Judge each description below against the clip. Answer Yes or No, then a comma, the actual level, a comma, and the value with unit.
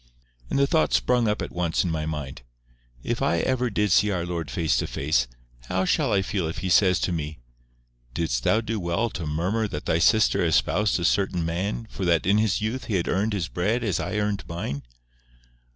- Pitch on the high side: No, very low, 90 Hz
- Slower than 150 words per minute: No, fast, 205 wpm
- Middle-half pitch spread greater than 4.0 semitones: Yes, average, 4.6 semitones